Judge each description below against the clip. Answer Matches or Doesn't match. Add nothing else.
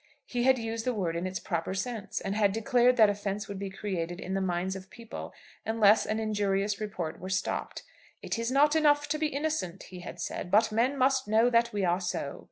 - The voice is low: Doesn't match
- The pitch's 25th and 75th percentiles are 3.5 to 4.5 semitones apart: Matches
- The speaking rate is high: Matches